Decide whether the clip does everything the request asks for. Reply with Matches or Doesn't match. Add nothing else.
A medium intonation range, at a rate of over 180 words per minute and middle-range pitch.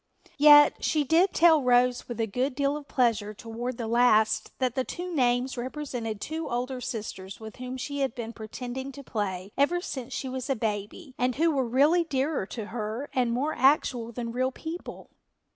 Doesn't match